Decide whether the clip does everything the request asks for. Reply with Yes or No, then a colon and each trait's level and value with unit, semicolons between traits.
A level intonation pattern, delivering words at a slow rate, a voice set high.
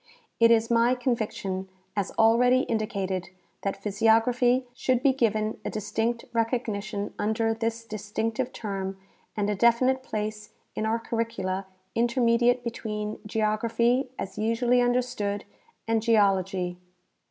Yes: narrow, 2.3 semitones; slow, 120 wpm; high, 225 Hz